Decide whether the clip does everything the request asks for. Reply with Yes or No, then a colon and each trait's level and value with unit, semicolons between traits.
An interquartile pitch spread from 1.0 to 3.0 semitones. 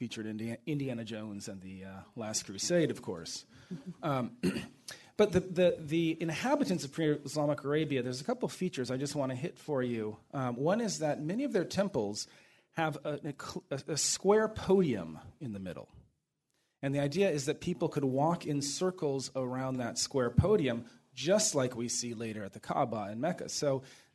No: average, 5.2 semitones